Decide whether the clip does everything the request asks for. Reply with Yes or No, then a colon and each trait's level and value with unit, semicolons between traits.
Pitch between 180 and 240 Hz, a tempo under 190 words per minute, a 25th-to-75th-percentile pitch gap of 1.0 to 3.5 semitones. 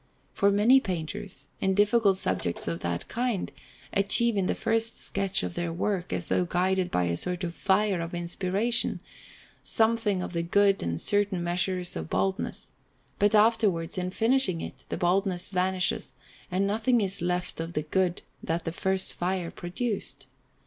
Yes: medium, 185 Hz; average, 165 wpm; average, 3.0 semitones